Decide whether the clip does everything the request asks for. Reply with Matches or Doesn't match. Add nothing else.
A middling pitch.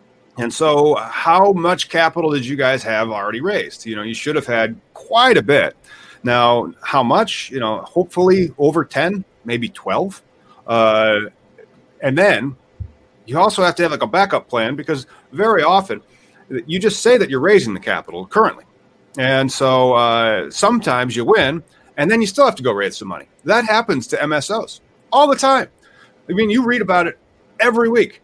Matches